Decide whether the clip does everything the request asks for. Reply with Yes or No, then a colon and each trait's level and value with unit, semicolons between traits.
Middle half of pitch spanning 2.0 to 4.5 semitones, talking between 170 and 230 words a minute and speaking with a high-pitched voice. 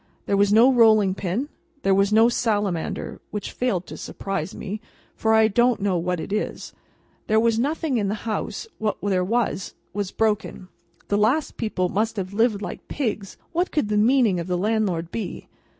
Yes: average, 2.7 semitones; average, 180 wpm; high, 210 Hz